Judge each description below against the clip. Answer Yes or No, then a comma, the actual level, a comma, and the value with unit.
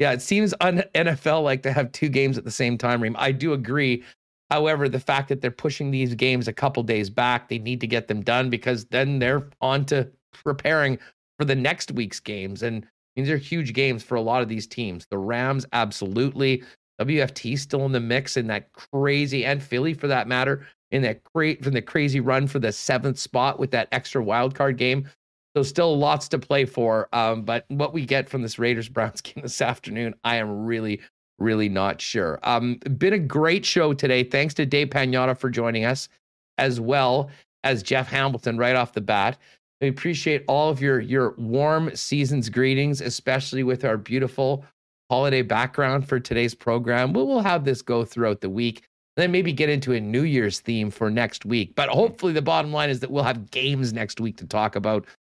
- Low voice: Yes, low, 130 Hz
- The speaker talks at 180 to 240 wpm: Yes, fast, 205 wpm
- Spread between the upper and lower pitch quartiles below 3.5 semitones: Yes, average, 3.0 semitones